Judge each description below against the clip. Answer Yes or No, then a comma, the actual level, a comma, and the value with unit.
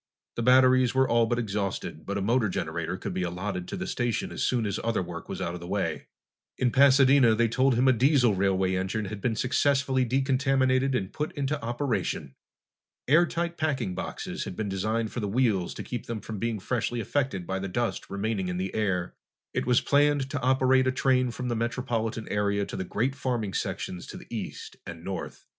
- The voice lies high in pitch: No, low, 120 Hz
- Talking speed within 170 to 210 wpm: Yes, fast, 205 wpm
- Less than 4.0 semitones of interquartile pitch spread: No, average, 4.7 semitones